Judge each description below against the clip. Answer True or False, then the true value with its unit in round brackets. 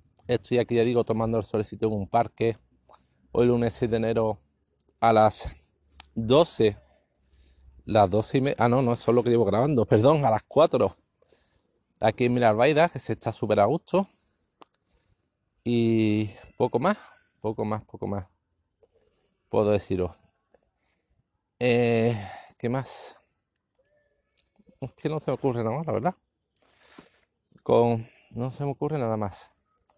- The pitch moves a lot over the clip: False (2.7 semitones)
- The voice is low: True (115 Hz)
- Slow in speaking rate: False (145 wpm)